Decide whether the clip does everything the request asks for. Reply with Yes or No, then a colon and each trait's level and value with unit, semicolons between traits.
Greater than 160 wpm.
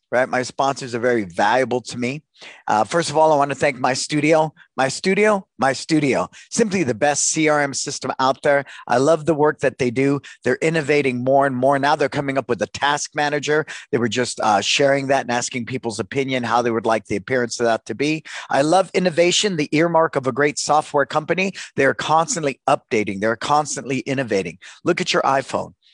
Yes: fast, 205 wpm